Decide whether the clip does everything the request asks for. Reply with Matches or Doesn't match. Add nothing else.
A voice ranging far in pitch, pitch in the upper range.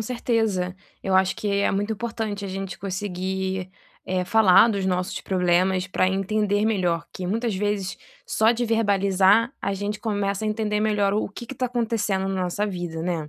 Doesn't match